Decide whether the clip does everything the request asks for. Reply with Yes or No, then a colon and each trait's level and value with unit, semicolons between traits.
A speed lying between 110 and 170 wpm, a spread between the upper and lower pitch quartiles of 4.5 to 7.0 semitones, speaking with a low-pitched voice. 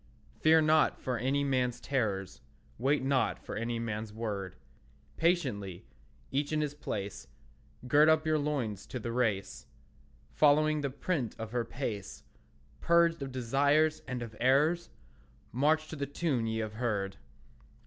Yes: average, 145 wpm; average, 5.2 semitones; low, 130 Hz